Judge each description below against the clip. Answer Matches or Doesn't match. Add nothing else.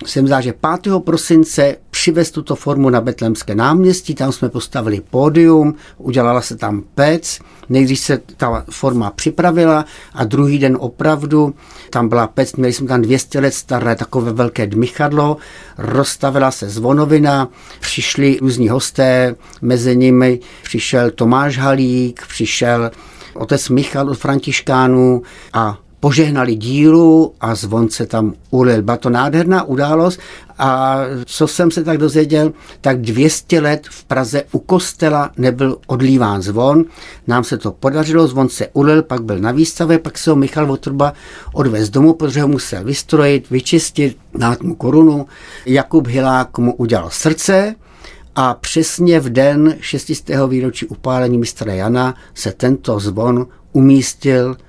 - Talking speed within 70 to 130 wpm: Doesn't match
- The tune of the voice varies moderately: Matches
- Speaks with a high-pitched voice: Doesn't match